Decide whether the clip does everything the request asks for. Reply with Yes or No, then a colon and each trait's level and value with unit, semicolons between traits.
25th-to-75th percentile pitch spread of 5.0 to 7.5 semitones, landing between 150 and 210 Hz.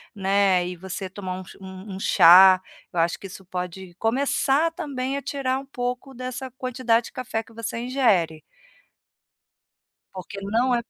No: average, 5.3 semitones; high, 220 Hz